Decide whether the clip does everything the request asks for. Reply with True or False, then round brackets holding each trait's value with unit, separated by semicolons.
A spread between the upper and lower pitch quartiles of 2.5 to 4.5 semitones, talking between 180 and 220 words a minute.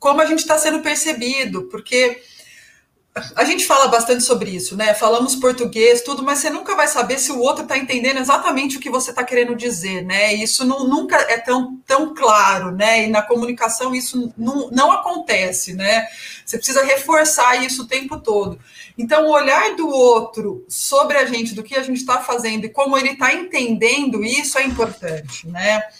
True (3.6 semitones; 185 wpm)